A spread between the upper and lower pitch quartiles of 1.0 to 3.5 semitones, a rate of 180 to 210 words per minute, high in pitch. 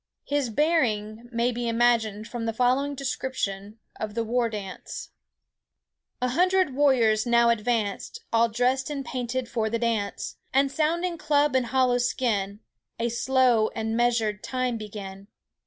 No: average, 3.0 semitones; average, 140 wpm; high, 240 Hz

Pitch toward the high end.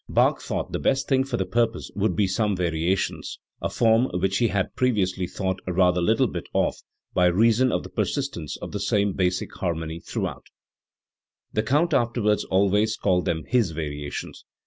No: low, 100 Hz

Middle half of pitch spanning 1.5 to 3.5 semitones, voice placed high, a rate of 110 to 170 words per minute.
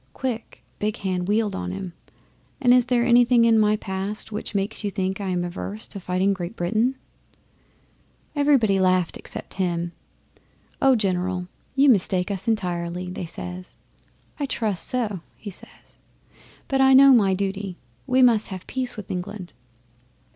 No: average, 4.3 semitones; high, 200 Hz; average, 155 wpm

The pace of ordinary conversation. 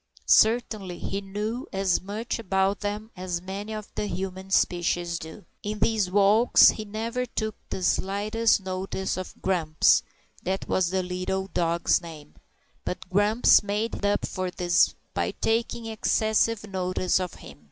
Yes: average, 145 wpm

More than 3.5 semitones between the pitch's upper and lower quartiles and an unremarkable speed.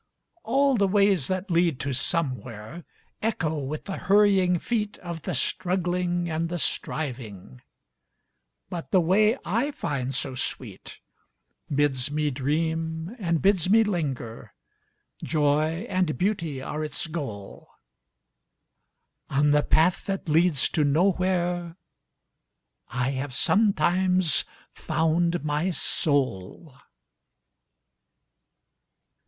No: average, 4.6 semitones; slow, 90 wpm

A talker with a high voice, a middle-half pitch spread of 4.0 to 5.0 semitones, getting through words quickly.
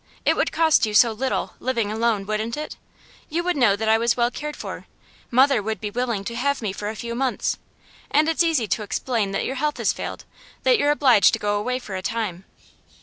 Yes: high, 235 Hz; average, 4.3 semitones; fast, 225 wpm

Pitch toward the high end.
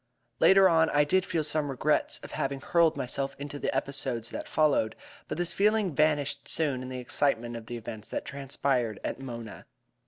No: medium, 140 Hz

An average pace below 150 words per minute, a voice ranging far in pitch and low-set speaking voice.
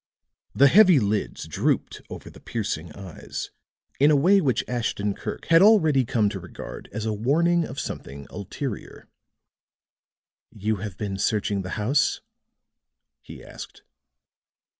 Yes: slow, 135 wpm; wide, 6.4 semitones; low, 110 Hz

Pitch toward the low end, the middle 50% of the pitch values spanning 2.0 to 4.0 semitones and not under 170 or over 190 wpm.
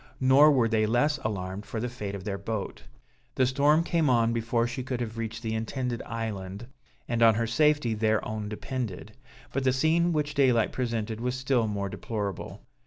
Yes: low, 115 Hz; average, 3.2 semitones; average, 185 wpm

